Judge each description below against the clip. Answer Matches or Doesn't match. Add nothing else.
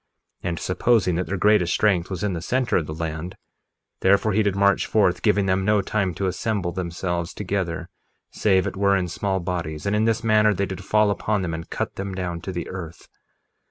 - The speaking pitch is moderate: Doesn't match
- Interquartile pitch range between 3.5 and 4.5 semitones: Doesn't match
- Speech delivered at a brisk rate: Matches